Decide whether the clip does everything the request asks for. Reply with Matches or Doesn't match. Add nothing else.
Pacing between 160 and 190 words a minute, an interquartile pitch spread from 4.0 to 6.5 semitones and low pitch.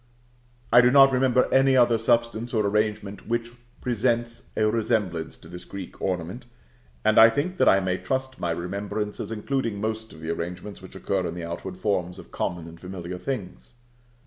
Matches